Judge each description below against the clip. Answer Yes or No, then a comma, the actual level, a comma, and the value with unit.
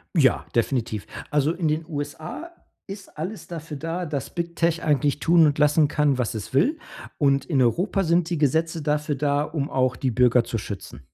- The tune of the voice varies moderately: Yes, average, 3.7 semitones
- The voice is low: No, medium, 150 Hz